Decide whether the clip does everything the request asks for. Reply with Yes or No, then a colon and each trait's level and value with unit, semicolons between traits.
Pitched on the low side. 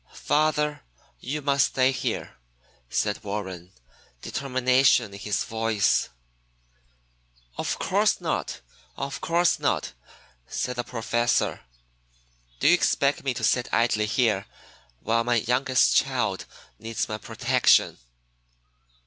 Yes: low, 120 Hz